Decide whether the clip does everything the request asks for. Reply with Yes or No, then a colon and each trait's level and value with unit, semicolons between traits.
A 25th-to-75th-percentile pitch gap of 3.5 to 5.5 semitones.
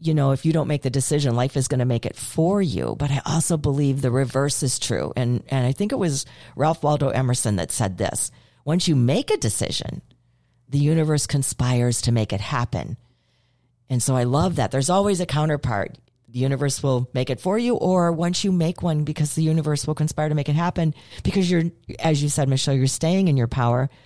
Yes: average, 4.1 semitones